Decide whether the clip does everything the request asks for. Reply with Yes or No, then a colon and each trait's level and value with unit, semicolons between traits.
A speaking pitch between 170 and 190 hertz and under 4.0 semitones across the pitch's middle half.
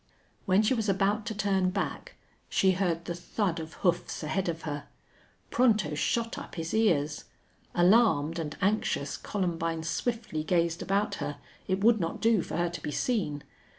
No: medium, 185 Hz; average, 4.3 semitones